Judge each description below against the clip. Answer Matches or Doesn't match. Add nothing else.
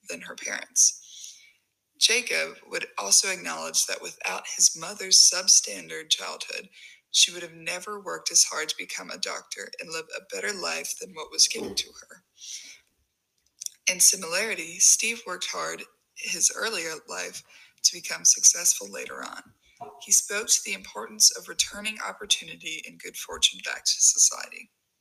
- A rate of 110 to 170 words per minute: Matches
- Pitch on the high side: Matches